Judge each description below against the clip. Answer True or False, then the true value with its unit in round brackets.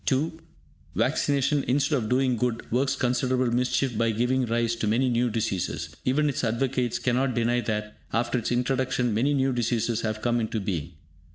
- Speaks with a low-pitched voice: True (120 Hz)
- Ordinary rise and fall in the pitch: False (2.3 semitones)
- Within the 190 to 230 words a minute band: False (170 wpm)